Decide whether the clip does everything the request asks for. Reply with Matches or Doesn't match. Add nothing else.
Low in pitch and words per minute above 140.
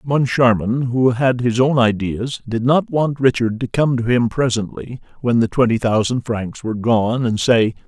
Matches